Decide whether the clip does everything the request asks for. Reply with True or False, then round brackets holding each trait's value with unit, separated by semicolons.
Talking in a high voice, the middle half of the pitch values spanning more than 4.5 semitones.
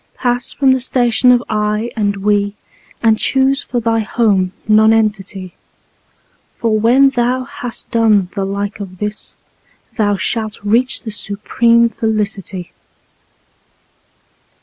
False (220 Hz; 2.8 semitones)